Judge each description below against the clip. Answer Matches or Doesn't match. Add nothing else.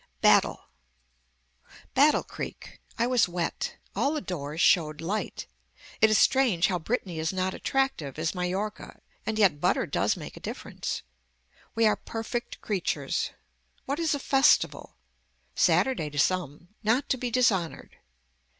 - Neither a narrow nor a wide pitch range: Doesn't match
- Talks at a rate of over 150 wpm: Doesn't match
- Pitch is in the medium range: Doesn't match